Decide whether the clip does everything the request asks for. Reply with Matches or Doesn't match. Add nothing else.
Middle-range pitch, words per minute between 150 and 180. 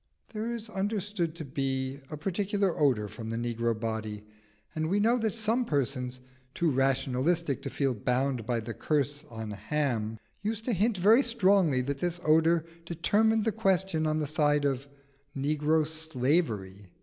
Matches